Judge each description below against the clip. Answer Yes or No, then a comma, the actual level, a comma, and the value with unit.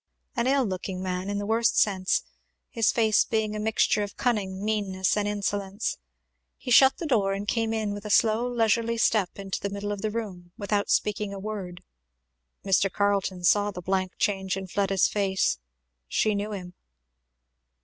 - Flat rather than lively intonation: Yes, narrow, 2.1 semitones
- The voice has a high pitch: Yes, high, 205 Hz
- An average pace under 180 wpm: Yes, average, 170 wpm